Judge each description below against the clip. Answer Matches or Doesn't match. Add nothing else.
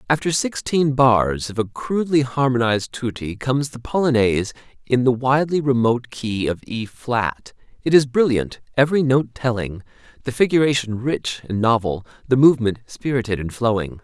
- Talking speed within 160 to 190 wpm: Doesn't match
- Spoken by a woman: Doesn't match